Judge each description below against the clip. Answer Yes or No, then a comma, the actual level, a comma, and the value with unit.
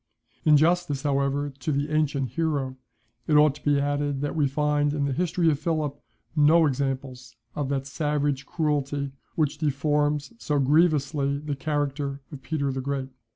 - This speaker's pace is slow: No, average, 160 wpm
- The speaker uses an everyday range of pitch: No, narrow, 1.6 semitones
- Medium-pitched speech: Yes, medium, 145 Hz